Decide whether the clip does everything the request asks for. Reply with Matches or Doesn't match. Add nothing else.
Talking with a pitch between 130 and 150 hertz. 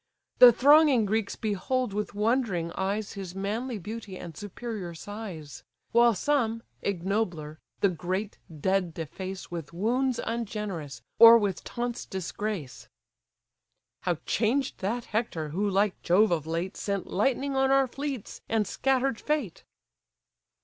Doesn't match